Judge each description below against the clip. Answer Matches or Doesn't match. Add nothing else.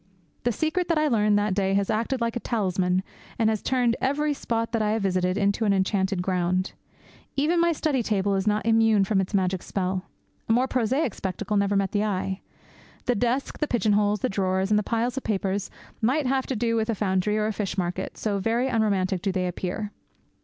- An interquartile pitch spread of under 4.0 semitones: Matches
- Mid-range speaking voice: Doesn't match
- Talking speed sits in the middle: Doesn't match